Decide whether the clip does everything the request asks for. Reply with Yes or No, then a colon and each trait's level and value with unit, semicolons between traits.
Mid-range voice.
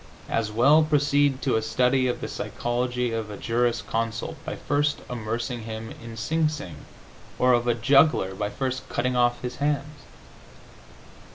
No: low, 125 Hz